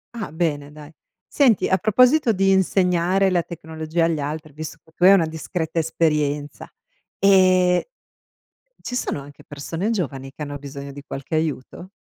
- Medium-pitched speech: Yes, medium, 165 Hz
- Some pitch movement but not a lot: Yes, average, 4.1 semitones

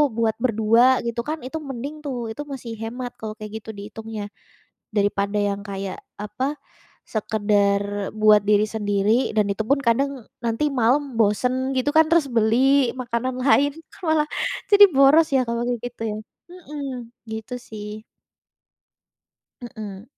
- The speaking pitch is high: Yes, high, 225 Hz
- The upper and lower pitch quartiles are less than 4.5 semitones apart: Yes, average, 3.7 semitones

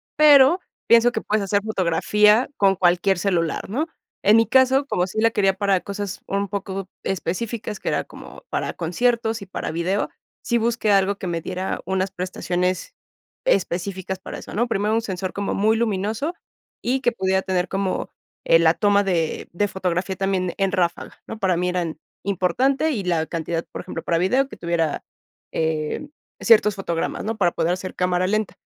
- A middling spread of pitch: Yes, average, 3.3 semitones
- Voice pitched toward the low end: No, high, 195 Hz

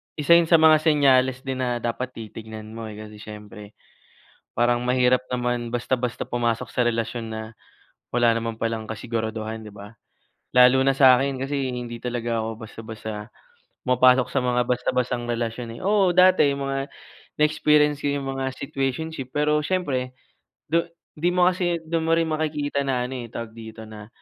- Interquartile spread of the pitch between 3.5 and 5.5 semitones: Yes, average, 3.8 semitones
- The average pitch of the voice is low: Yes, low, 125 Hz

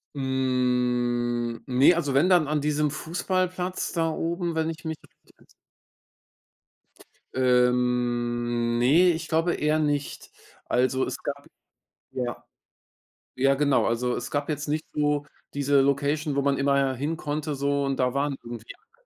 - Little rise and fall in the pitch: No, average, 3.6 semitones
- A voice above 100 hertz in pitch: Yes, medium, 140 Hz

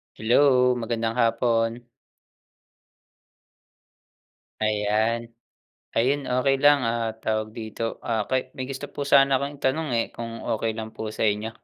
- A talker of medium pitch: No, low, 115 Hz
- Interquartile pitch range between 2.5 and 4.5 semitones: Yes, average, 2.9 semitones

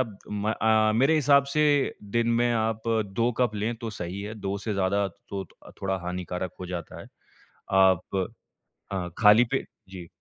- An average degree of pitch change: Yes, average, 3.4 semitones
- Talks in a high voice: No, low, 105 Hz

